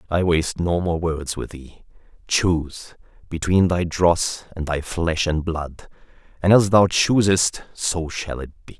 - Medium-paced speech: Yes, average, 155 wpm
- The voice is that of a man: Yes, male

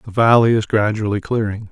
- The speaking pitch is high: No, low, 110 Hz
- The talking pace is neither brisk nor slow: Yes, average, 175 wpm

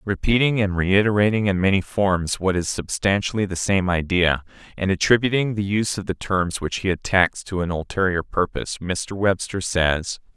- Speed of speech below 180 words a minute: Yes, average, 170 wpm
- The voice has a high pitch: No, very low, 95 Hz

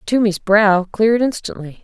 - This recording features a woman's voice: Yes, female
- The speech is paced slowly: Yes, slow, 130 wpm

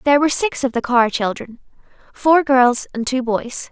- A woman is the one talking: Yes, female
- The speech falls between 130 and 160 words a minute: No, average, 180 wpm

